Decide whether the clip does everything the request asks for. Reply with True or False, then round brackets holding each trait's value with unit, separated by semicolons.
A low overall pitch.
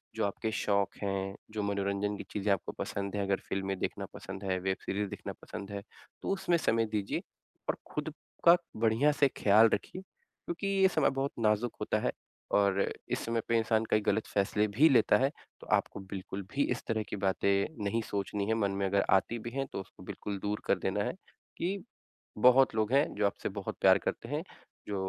True (105 Hz)